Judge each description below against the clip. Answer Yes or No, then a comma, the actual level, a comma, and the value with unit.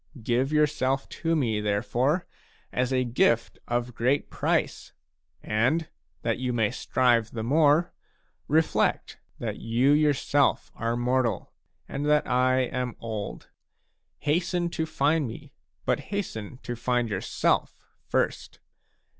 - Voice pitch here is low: Yes, low, 130 Hz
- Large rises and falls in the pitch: No, average, 4.1 semitones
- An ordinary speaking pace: No, slow, 120 wpm